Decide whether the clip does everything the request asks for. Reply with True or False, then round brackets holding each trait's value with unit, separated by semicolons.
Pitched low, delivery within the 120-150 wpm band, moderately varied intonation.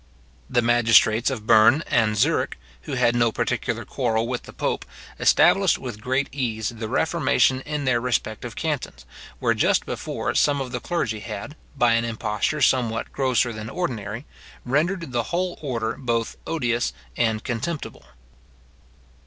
True (120 Hz; 145 wpm; 3.2 semitones)